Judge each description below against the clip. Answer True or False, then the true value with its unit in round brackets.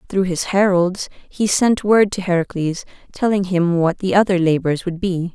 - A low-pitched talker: False (185 Hz)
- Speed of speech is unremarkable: True (180 wpm)